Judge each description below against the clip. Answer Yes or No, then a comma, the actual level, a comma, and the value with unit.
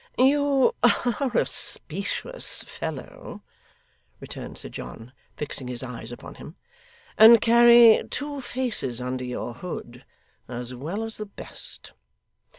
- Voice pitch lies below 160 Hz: No, high, 205 Hz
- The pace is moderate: No, slow, 120 wpm